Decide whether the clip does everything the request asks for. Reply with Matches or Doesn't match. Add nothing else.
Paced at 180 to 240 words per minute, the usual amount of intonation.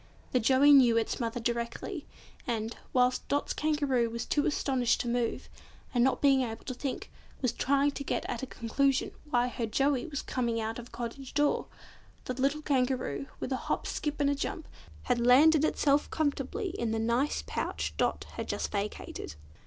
Matches